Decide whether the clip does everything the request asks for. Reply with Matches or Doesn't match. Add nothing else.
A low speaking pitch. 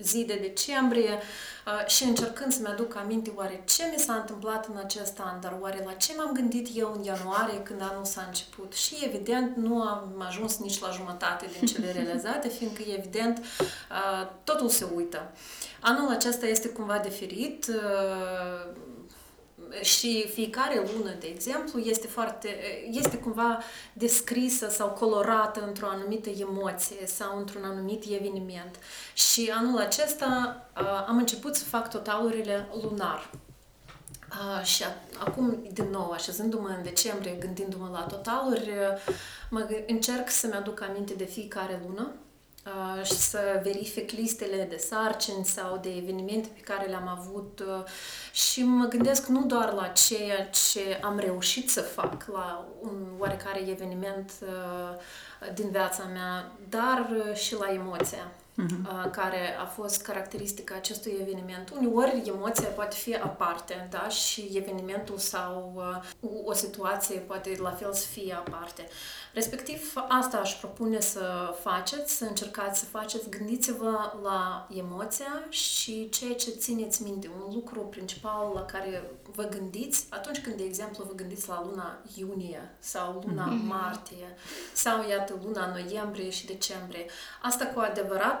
Doesn't match